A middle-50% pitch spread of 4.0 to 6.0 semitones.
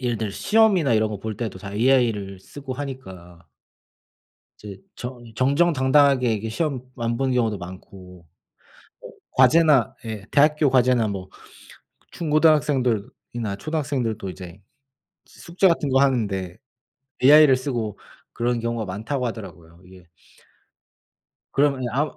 Yes: wide, 5.4 semitones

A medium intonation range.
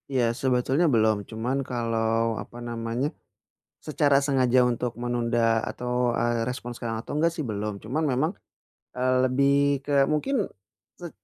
Yes: average, 3.1 semitones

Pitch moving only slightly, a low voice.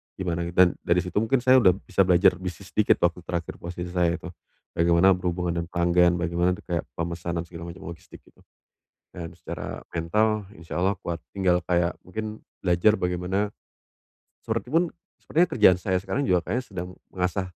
Yes: narrow, 1.9 semitones; very low, 90 Hz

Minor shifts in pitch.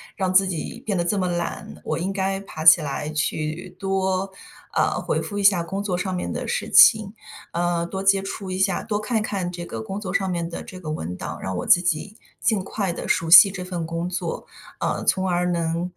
Yes: narrow, 2.3 semitones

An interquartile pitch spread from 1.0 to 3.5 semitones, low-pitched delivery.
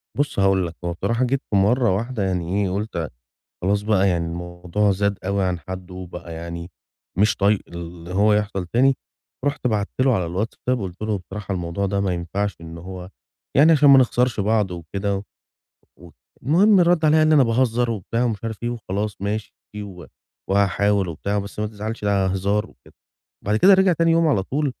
No: average, 4.1 semitones; low, 100 Hz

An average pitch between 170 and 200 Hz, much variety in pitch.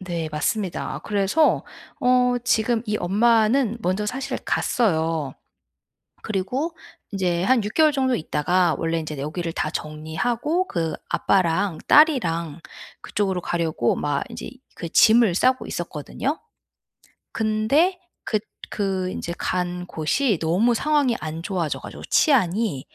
Yes: high, 195 Hz; wide, 6.7 semitones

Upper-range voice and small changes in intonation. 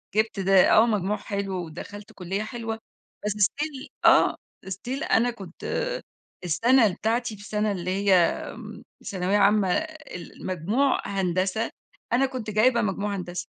No: high, 210 Hz; average, 3.5 semitones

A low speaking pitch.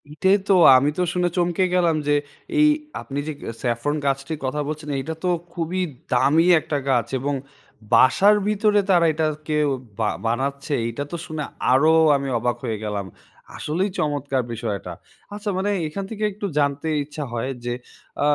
No: medium, 150 Hz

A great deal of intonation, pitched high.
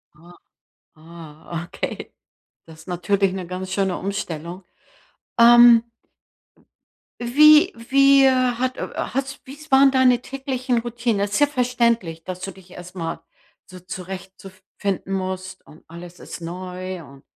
Yes: wide, 5.7 semitones; high, 195 Hz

